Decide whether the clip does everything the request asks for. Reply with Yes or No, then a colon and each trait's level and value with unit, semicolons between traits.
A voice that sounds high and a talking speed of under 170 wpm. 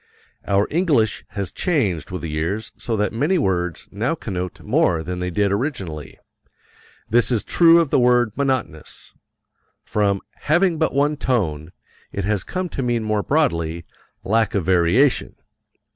No: low, 105 Hz; average, 150 wpm